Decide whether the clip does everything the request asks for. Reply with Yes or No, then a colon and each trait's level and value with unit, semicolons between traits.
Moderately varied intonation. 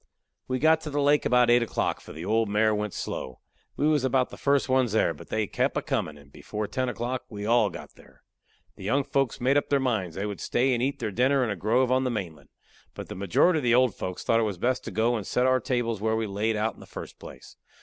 Yes: average, 3.6 semitones